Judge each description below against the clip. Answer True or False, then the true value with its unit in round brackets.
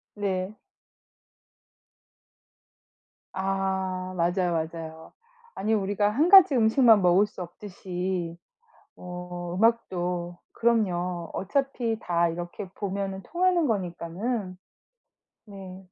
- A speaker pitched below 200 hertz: True (190 Hz)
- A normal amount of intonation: True (3.4 semitones)